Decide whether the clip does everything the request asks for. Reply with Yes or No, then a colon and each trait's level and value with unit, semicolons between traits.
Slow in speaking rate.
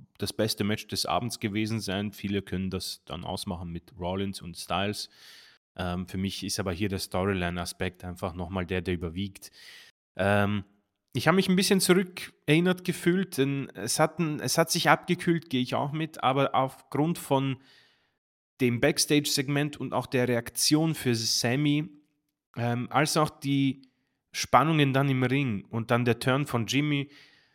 No: average, 160 wpm